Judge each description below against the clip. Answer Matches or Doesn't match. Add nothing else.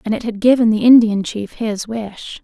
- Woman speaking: Matches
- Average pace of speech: Doesn't match